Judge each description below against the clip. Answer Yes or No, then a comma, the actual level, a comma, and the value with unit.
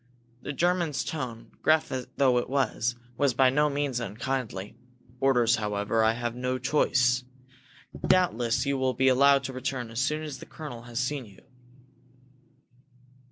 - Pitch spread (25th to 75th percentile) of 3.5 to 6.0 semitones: No, average, 2.9 semitones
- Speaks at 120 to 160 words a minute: Yes, average, 150 wpm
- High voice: No, low, 130 Hz